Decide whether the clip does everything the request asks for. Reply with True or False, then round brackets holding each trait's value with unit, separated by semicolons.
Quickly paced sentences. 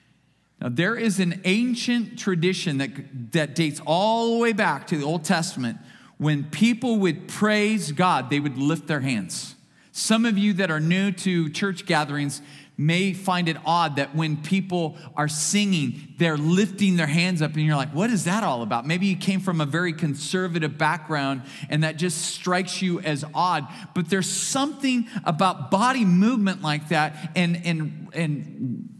False (180 wpm)